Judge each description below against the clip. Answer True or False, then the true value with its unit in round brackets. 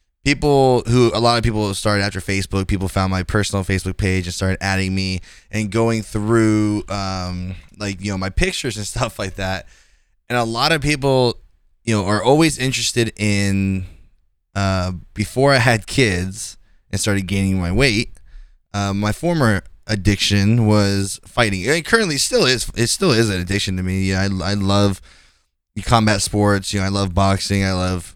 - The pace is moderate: True (180 wpm)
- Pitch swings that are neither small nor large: True (3.1 semitones)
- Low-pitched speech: True (100 Hz)